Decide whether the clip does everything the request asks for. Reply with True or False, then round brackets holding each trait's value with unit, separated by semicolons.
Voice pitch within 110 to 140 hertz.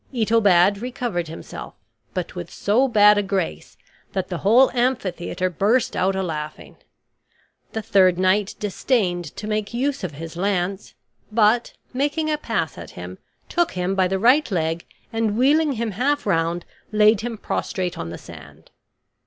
False (200 Hz)